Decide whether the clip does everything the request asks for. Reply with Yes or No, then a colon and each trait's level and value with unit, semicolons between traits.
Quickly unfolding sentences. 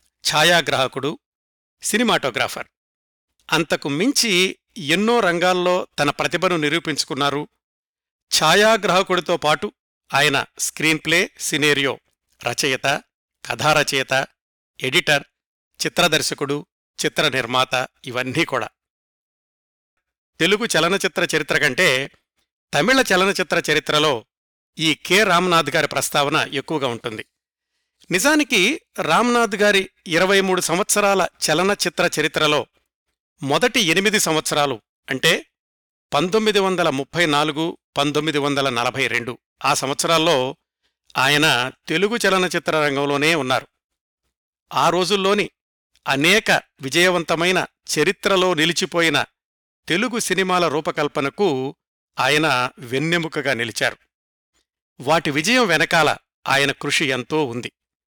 No: average, 85 wpm